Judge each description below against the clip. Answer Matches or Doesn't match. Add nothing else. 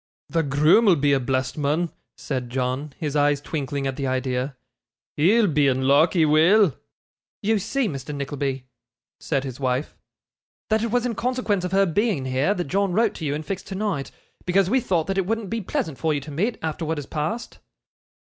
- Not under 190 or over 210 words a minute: Matches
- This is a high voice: Doesn't match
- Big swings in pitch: Matches